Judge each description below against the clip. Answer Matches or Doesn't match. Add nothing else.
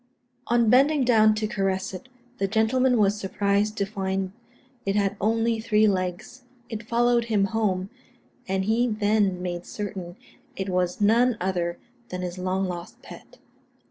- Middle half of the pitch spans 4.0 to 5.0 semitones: Doesn't match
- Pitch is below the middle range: Doesn't match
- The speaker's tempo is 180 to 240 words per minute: Doesn't match